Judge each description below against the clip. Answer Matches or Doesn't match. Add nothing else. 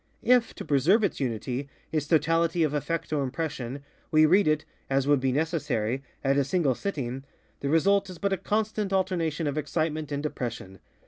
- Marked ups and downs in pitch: Doesn't match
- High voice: Doesn't match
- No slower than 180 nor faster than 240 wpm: Doesn't match